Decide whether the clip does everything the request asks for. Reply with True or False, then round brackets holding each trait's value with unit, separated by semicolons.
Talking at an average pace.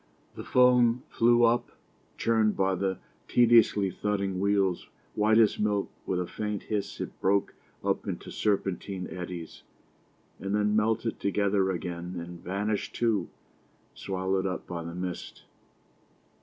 False (130 wpm)